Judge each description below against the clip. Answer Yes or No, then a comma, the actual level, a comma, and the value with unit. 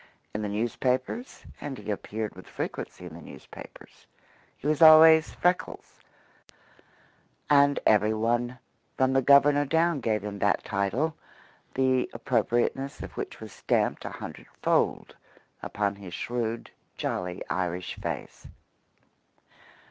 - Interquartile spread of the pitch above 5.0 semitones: Yes, wide, 5.5 semitones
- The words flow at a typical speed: No, slow, 125 wpm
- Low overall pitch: Yes, low, 120 Hz